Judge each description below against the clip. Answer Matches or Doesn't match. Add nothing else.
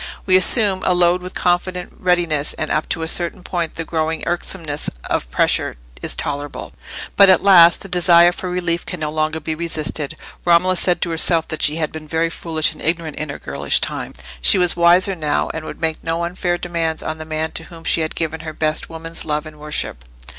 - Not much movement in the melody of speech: Matches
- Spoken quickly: Matches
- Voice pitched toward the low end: Doesn't match